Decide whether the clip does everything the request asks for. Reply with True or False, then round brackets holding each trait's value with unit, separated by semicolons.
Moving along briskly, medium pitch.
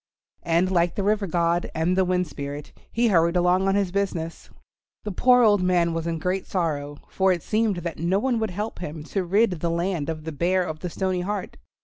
True (215 wpm; 180 Hz)